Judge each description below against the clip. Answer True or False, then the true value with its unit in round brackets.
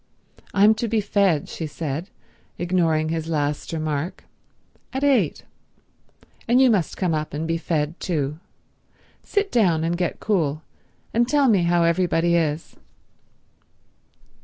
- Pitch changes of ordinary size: True (4.6 semitones)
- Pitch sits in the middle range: True (170 Hz)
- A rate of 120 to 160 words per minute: True (135 wpm)